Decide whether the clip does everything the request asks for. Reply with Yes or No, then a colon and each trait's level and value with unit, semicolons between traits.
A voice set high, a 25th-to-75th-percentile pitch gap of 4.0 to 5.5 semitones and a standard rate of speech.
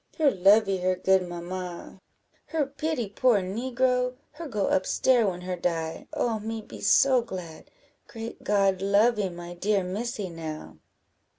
Yes: high, 200 Hz; average, 4.7 semitones; average, 150 wpm